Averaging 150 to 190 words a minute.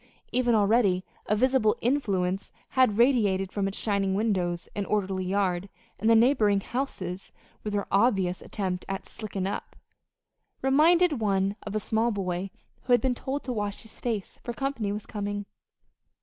Yes: average, 160 wpm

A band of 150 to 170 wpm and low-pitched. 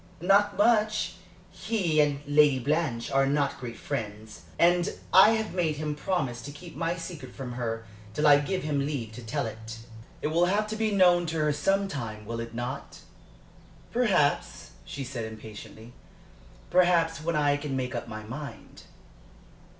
No: average, 165 wpm; medium, 150 Hz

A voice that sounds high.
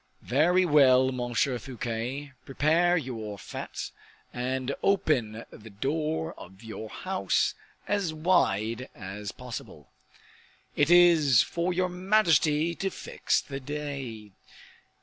No: medium, 140 Hz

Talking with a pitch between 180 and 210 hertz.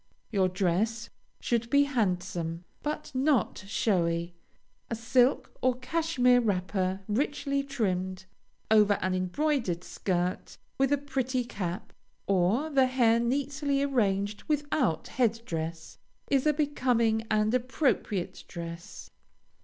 No: high, 230 Hz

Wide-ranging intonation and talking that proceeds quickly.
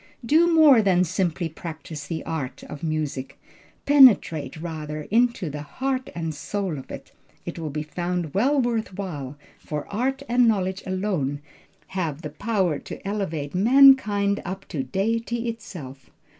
No: wide, 6.8 semitones; average, 145 wpm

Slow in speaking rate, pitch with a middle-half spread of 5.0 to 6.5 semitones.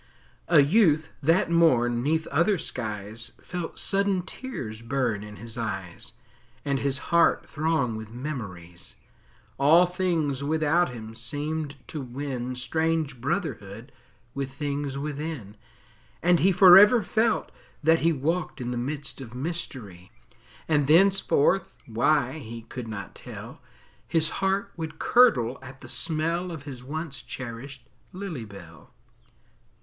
Yes: slow, 130 wpm; average, 5.3 semitones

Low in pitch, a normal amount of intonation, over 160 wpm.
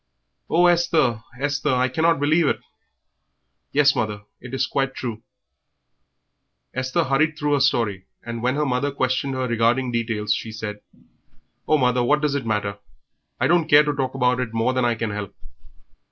Yes: low, 130 Hz; average, 3.8 semitones; average, 170 wpm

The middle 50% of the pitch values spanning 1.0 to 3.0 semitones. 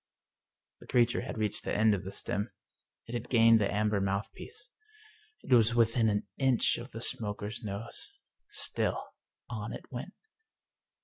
Yes: narrow, 2.6 semitones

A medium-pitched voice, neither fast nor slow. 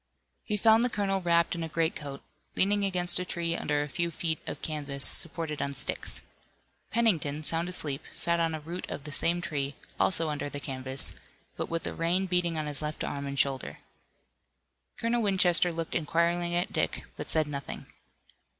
Yes: medium, 165 Hz; average, 180 wpm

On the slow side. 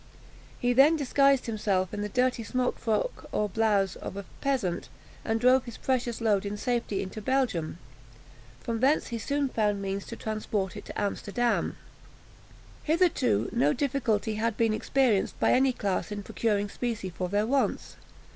No: average, 160 wpm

